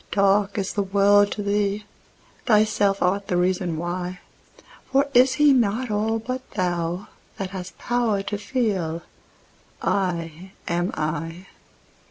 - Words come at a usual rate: No, slow, 125 wpm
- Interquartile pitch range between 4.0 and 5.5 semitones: No, average, 3.0 semitones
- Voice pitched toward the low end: No, high, 200 Hz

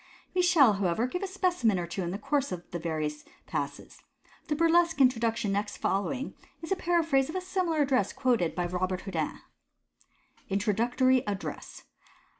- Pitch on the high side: Yes, high, 245 Hz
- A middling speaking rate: Yes, average, 170 wpm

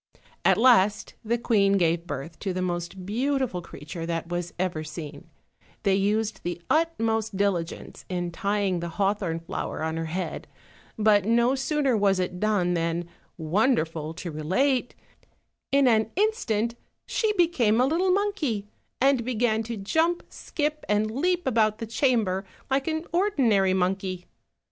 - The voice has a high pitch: Yes, high, 210 Hz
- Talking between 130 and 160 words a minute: Yes, average, 150 wpm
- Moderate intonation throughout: No, wide, 6.2 semitones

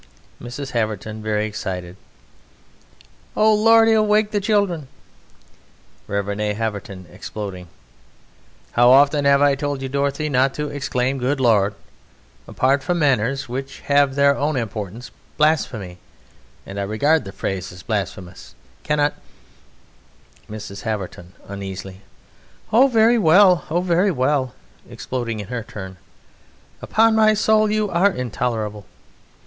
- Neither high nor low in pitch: No, low, 130 Hz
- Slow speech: Yes, slow, 125 wpm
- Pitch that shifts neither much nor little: No, wide, 6.9 semitones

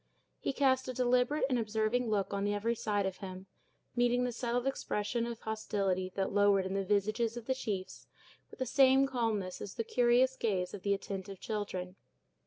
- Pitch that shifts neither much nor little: Yes, average, 3.8 semitones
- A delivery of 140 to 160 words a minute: No, average, 185 wpm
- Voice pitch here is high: Yes, high, 220 Hz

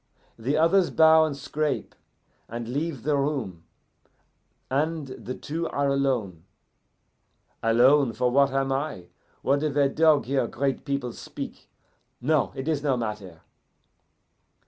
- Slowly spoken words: Yes, slow, 130 wpm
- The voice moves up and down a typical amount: Yes, average, 3.6 semitones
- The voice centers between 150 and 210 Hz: No, medium, 140 Hz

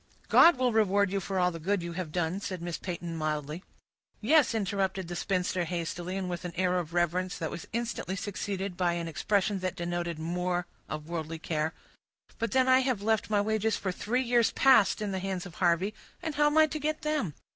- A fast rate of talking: Yes, fast, 210 wpm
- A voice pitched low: No, medium, 185 Hz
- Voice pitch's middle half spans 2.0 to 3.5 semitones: No, average, 3.9 semitones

